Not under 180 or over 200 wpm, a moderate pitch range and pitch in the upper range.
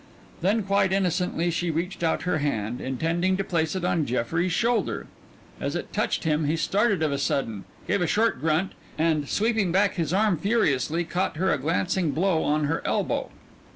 No: average, 185 wpm; average, 3.7 semitones; medium, 170 Hz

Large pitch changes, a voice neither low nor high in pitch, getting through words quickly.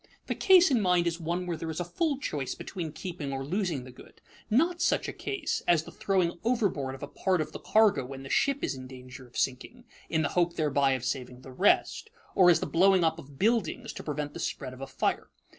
Yes: wide, 6.2 semitones; medium, 165 Hz; fast, 240 wpm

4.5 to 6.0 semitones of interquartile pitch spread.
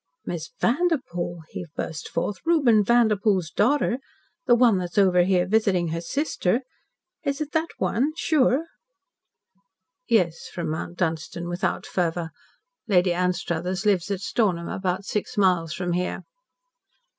Yes: average, 5.1 semitones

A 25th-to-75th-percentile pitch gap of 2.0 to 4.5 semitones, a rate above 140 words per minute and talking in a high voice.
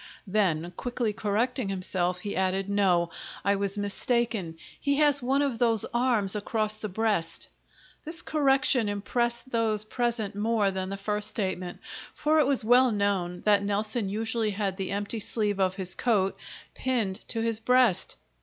Yes: average, 3.5 semitones; average, 155 wpm; high, 210 Hz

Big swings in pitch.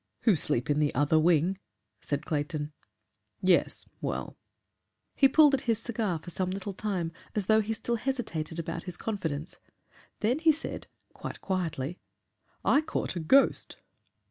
Yes: wide, 6.2 semitones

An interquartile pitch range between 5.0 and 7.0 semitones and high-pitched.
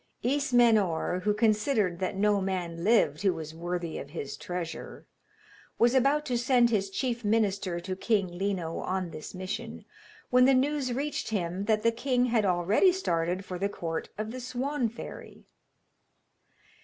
Yes: average, 5.3 semitones; high, 205 Hz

